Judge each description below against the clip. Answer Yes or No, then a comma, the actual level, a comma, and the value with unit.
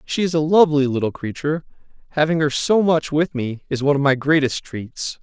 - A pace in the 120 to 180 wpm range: No, fast, 205 wpm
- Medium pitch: Yes, medium, 145 Hz